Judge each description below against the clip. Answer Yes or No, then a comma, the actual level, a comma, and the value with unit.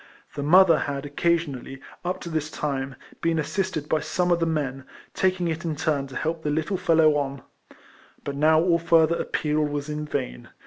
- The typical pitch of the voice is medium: Yes, medium, 155 Hz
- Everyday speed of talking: Yes, average, 180 wpm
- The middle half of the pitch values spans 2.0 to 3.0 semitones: Yes, average, 2.7 semitones